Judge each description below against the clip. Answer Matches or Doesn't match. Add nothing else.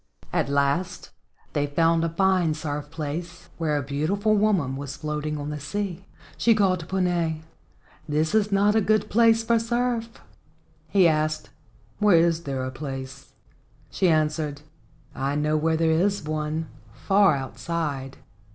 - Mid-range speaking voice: Matches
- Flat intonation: Doesn't match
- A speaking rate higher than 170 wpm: Doesn't match